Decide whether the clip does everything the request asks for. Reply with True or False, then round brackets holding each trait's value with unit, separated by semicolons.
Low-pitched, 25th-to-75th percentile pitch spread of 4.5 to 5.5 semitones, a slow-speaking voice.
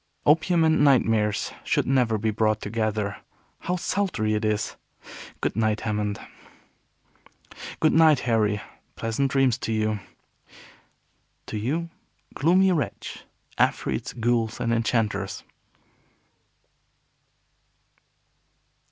True (115 Hz; 4.8 semitones; 95 wpm)